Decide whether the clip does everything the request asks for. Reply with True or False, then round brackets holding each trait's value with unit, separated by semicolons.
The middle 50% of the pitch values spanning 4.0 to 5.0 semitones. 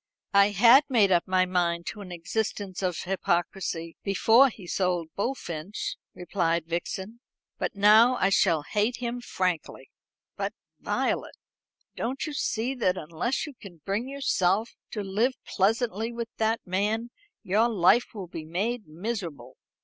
True (4.6 semitones)